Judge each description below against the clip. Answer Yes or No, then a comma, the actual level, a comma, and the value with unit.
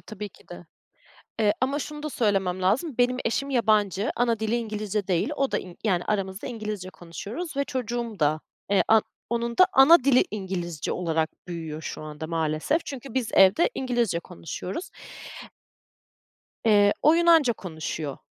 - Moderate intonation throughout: No, wide, 5.8 semitones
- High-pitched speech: Yes, high, 215 Hz